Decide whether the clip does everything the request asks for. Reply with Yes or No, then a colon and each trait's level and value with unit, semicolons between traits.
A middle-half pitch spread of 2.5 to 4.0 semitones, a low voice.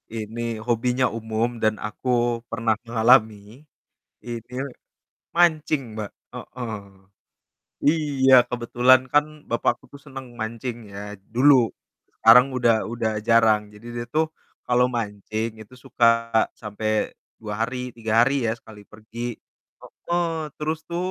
Yes: average, 3.0 semitones; low, 120 Hz